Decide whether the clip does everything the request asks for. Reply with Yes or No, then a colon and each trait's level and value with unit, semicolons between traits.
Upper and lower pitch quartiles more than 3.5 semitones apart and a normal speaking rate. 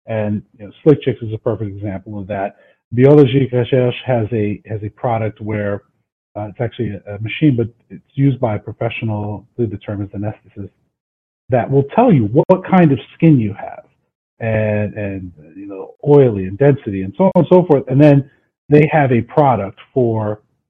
Yes: average, 4.7 semitones; average, 185 wpm